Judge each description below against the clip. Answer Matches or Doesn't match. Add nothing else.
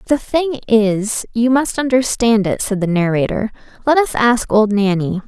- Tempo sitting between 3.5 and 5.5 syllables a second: Matches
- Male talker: Doesn't match